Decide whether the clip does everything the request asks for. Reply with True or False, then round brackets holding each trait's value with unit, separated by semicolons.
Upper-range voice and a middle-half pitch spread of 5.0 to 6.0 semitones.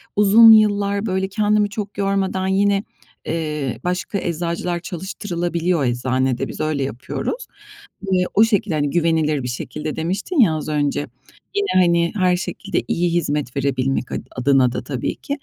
False (175 Hz; 5.4 semitones)